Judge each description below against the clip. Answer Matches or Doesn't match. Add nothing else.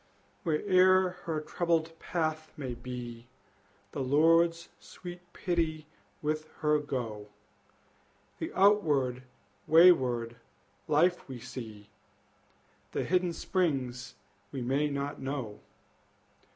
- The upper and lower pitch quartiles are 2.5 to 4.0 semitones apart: Doesn't match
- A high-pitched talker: Doesn't match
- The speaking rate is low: Matches